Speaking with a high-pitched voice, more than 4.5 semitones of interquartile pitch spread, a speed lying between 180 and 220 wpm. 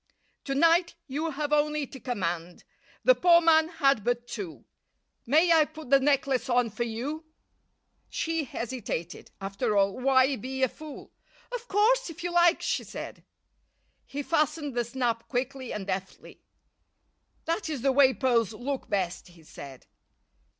No: very high, 265 Hz; average, 5.3 semitones; average, 150 wpm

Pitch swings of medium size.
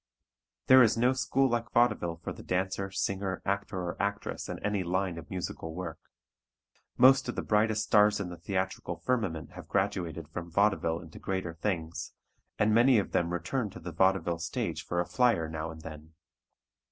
Yes: average, 4.0 semitones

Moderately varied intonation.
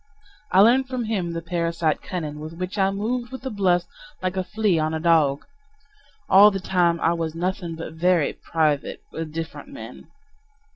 Yes: average, 3.4 semitones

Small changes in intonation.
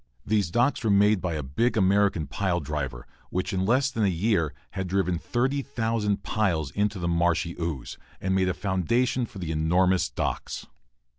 No: average, 4.1 semitones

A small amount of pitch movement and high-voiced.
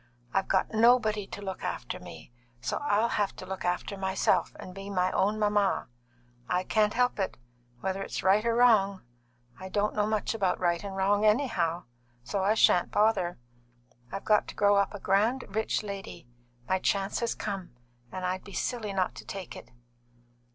Yes: narrow, 2.1 semitones; high, 200 Hz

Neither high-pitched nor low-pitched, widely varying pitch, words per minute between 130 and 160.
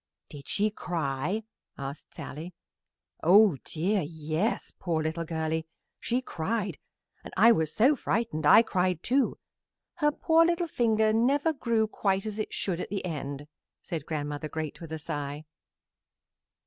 Yes: medium, 180 Hz; wide, 6.0 semitones; average, 145 wpm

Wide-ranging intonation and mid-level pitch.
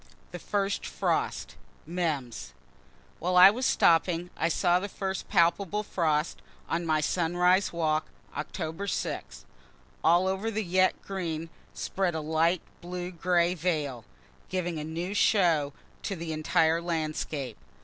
No: narrow, 2.6 semitones; medium, 170 Hz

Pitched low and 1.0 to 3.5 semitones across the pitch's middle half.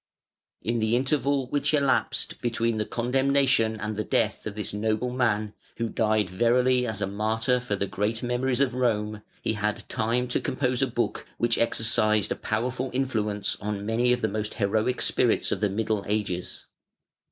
Yes: low, 115 Hz; average, 2.7 semitones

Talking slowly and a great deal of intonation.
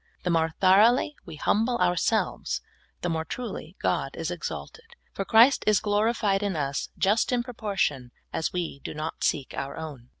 No: average, 165 wpm; wide, 5.8 semitones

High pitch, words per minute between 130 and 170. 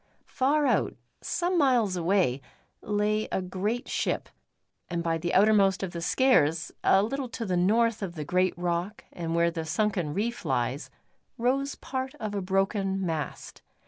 Yes: high, 195 Hz; average, 160 wpm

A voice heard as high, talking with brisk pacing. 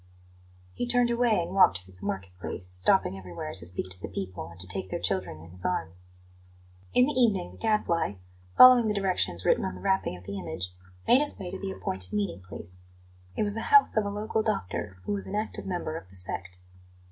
No: low, 105 Hz; fast, 220 wpm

